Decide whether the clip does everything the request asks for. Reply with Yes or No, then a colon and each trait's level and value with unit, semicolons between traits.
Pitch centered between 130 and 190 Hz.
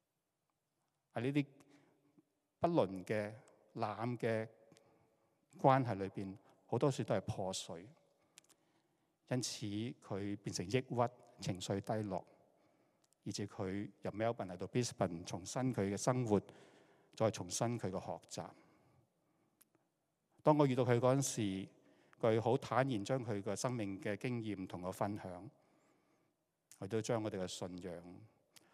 No: low, 110 Hz